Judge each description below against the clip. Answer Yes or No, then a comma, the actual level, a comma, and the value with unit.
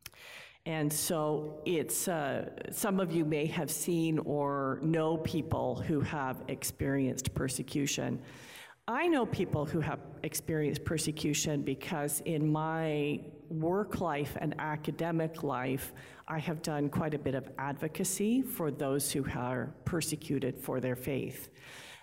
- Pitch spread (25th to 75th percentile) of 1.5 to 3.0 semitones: Yes, narrow, 2.5 semitones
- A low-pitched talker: No, medium, 150 Hz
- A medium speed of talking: No, slow, 130 wpm